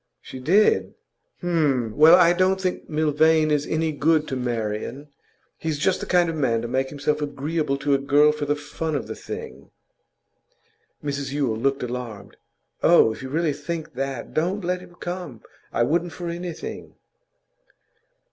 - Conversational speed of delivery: Yes, average, 165 wpm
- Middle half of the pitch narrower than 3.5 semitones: No, average, 3.8 semitones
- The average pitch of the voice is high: No, medium, 150 Hz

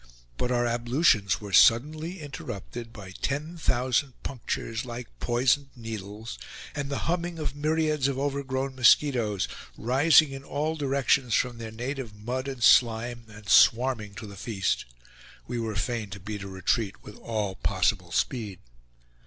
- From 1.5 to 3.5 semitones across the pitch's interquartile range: No, average, 4.3 semitones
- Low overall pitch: Yes, low, 120 Hz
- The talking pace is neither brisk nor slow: Yes, average, 150 wpm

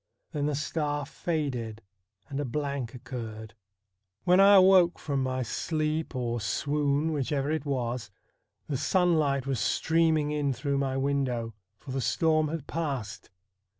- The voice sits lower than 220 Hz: Yes, medium, 140 Hz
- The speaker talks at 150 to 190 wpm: No, average, 140 wpm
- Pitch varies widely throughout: No, average, 3.2 semitones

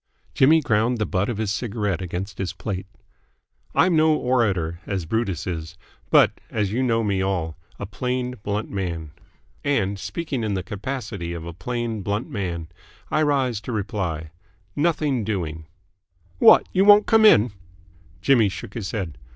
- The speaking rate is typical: Yes, average, 160 wpm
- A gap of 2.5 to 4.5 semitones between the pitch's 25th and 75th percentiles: No, average, 5.1 semitones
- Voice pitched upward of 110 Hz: No, low, 105 Hz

